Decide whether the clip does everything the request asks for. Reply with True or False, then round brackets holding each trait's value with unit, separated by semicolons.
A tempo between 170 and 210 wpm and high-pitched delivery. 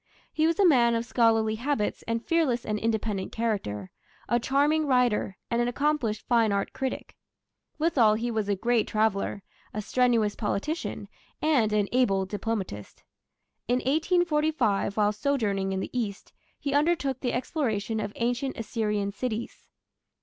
False (145 wpm; 230 Hz)